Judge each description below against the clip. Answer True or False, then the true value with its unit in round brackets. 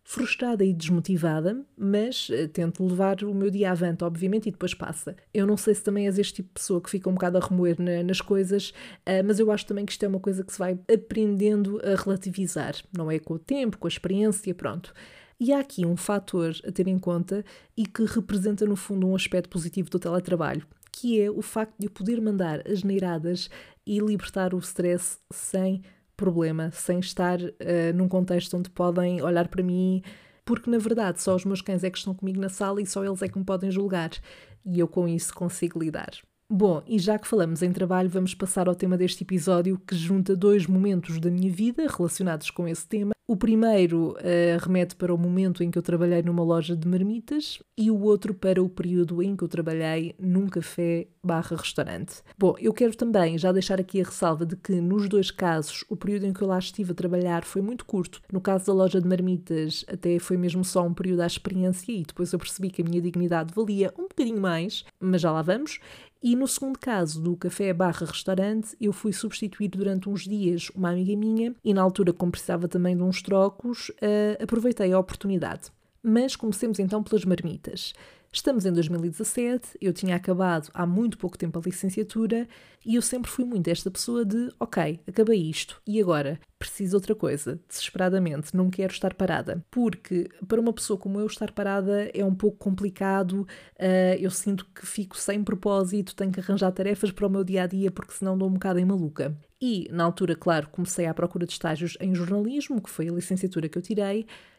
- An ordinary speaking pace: False (205 wpm)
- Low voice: False (190 Hz)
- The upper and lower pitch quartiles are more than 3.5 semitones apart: False (2.6 semitones)